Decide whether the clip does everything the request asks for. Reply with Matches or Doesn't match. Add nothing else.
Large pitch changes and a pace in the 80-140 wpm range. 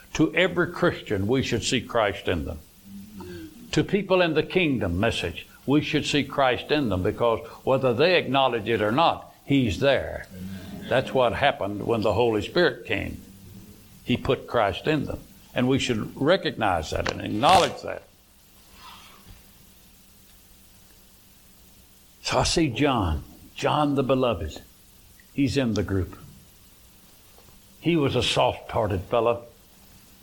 Matches